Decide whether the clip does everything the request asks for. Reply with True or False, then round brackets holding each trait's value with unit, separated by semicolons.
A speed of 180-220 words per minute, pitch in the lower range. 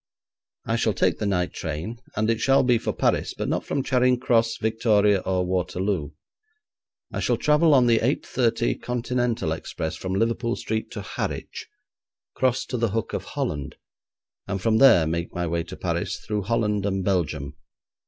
False (170 wpm; 105 Hz)